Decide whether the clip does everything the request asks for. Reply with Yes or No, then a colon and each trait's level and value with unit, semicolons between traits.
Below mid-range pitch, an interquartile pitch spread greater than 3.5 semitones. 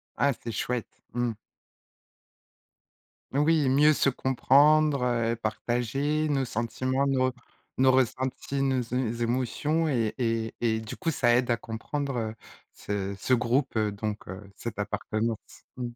No: low, 125 Hz; average, 3.2 semitones